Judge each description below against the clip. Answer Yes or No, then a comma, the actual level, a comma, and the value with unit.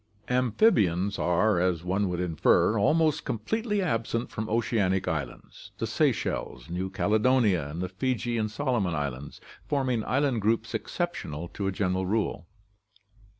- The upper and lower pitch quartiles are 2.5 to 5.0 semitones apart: No, wide, 5.5 semitones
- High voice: No, low, 105 Hz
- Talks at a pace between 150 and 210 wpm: No, slow, 135 wpm